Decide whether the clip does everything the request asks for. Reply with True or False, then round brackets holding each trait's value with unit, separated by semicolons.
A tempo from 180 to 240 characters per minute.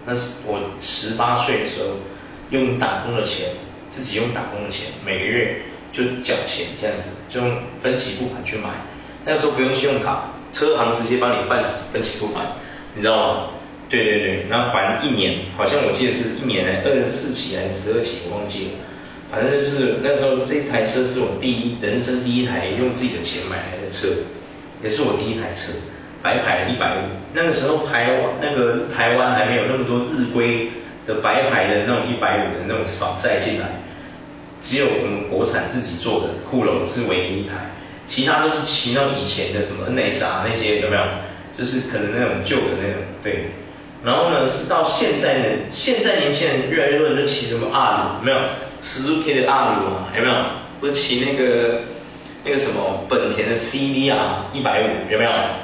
False (290 characters per minute)